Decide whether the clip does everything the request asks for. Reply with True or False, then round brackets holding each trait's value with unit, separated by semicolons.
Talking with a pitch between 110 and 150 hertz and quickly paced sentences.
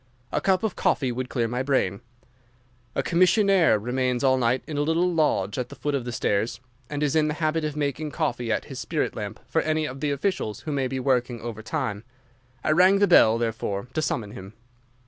True (135 Hz; 215 wpm)